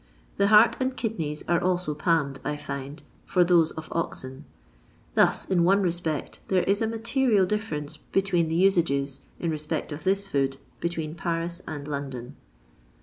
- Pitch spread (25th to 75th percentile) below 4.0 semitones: No, average, 4.6 semitones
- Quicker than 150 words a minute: Yes, average, 165 wpm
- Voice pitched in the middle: Yes, medium, 170 Hz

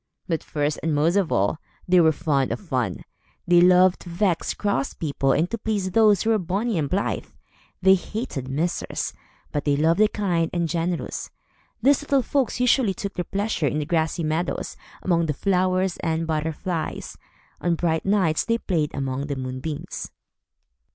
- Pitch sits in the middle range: Yes, medium, 170 Hz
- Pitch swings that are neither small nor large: Yes, average, 4.2 semitones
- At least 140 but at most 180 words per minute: Yes, average, 170 wpm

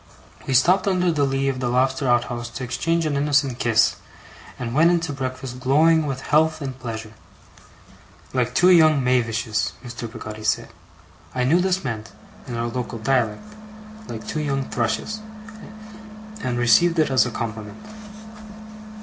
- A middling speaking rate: Yes, average, 155 wpm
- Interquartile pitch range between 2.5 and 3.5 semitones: No, average, 4.4 semitones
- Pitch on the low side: Yes, low, 130 Hz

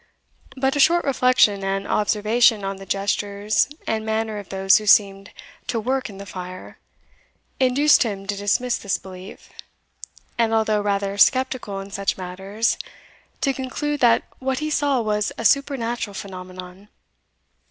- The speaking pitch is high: Yes, high, 210 Hz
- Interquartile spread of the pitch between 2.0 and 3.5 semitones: No, average, 4.3 semitones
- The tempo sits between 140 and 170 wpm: Yes, average, 145 wpm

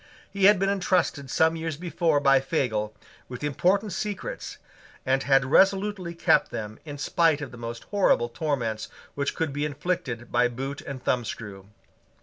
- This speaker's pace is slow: No, average, 155 wpm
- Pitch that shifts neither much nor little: No, wide, 5.8 semitones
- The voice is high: No, medium, 145 Hz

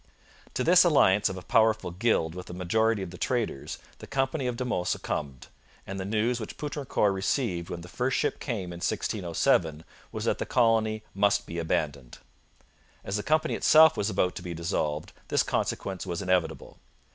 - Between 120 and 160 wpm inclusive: No, average, 180 wpm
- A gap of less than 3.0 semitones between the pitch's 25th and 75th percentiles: No, average, 5.2 semitones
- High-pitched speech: No, low, 100 Hz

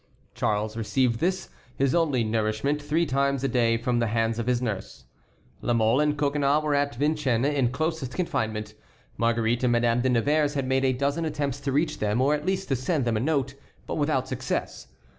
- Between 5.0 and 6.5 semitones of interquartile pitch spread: No, average, 3.9 semitones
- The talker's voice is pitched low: Yes, low, 130 Hz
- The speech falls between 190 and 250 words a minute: Yes, average, 200 wpm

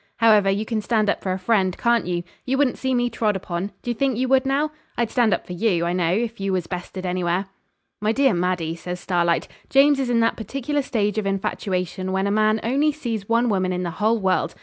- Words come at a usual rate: No, fast, 235 wpm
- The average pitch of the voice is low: No, high, 210 Hz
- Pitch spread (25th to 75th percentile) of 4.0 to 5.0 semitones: Yes, average, 4.6 semitones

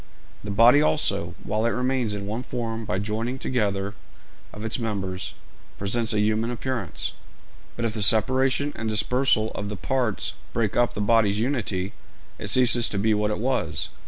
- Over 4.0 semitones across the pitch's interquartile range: No, average, 2.8 semitones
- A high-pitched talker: No, low, 110 Hz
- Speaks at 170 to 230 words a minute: Yes, average, 175 wpm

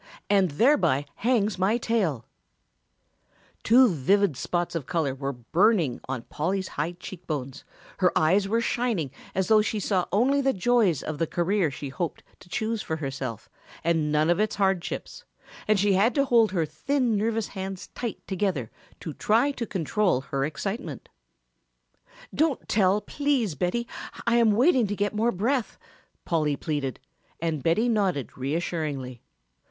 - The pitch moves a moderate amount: No, wide, 6.2 semitones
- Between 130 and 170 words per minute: Yes, average, 155 wpm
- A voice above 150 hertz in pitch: Yes, high, 190 Hz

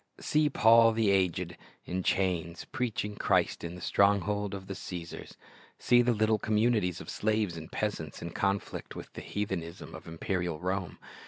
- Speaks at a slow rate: No, average, 160 wpm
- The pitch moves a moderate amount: Yes, average, 3.6 semitones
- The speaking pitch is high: No, low, 100 Hz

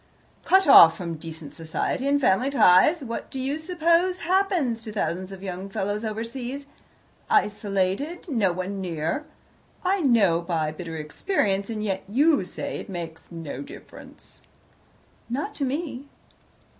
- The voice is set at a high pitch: Yes, high, 215 Hz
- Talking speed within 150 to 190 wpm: No, average, 140 wpm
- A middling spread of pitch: No, wide, 7.9 semitones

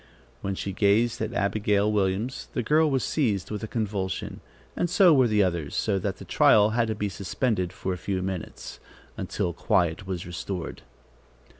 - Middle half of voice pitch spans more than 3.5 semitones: No, average, 3.1 semitones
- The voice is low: Yes, low, 100 Hz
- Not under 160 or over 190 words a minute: Yes, average, 175 wpm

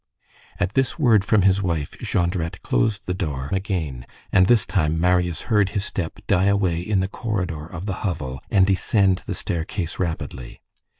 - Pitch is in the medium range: No, very low, 90 Hz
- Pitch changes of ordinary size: Yes, average, 3.3 semitones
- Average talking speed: Yes, average, 170 wpm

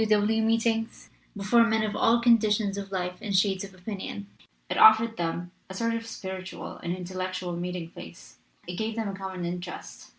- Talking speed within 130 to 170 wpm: No, average, 185 wpm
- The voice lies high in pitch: Yes, high, 195 Hz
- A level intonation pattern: No, average, 3.6 semitones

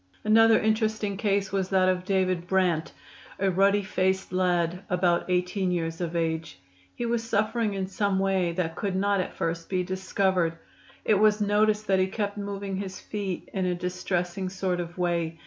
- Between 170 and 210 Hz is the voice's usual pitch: Yes, high, 190 Hz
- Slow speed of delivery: No, average, 175 wpm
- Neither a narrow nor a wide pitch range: No, narrow, 2.1 semitones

